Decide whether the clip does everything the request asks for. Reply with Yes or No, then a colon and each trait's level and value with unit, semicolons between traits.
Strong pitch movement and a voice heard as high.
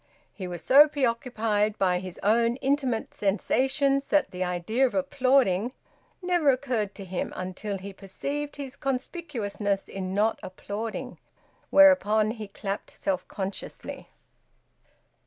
Yes: wide, 5.7 semitones; high, 220 Hz